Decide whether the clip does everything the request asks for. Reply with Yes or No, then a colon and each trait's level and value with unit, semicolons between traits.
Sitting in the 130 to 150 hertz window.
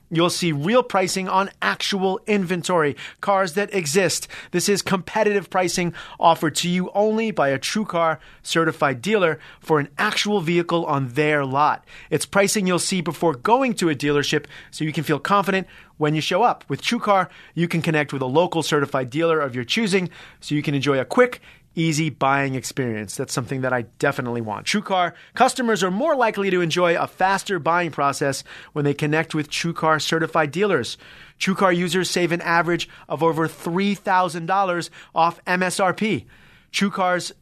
No: medium, 170 Hz